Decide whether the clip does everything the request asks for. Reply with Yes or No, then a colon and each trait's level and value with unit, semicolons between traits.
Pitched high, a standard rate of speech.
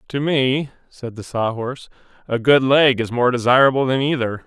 No: low, 130 Hz; average, 190 wpm